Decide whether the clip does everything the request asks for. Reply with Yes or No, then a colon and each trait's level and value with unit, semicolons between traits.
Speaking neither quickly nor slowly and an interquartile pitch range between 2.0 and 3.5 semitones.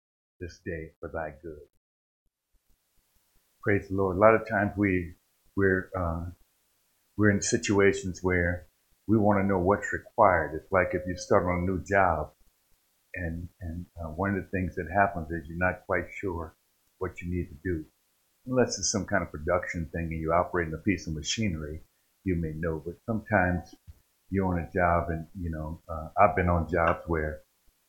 Yes: average, 185 wpm; average, 2.9 semitones